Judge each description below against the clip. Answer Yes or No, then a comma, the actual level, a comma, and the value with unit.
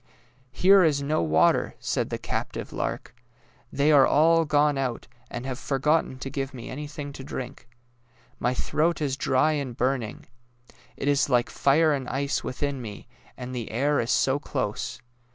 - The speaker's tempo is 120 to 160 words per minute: No, average, 170 wpm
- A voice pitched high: No, low, 135 Hz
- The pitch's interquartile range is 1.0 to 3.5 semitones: Yes, average, 2.7 semitones